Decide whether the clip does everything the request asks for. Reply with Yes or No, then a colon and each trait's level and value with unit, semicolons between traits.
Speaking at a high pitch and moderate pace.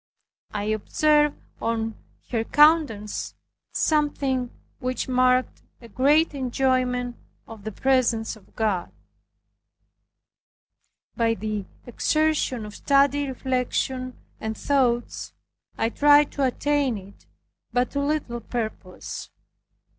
No: very high, 255 Hz; slow, 100 wpm